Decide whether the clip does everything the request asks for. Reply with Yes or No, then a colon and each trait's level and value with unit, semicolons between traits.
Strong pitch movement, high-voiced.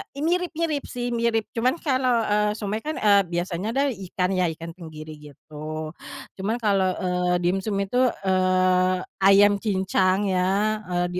No: average, 3.7 semitones; high, 195 Hz